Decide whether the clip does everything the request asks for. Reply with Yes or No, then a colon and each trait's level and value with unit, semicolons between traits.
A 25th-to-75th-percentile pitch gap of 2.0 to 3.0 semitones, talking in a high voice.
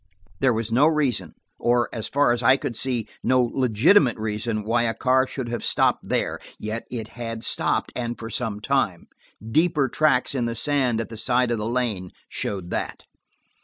No: narrow, 2.6 semitones; low, 120 Hz